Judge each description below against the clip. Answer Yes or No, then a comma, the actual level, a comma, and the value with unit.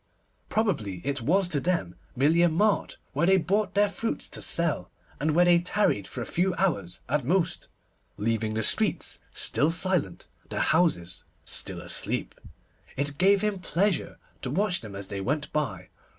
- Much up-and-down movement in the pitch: Yes, wide, 8.2 semitones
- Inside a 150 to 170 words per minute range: Yes, average, 165 wpm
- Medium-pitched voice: Yes, medium, 160 Hz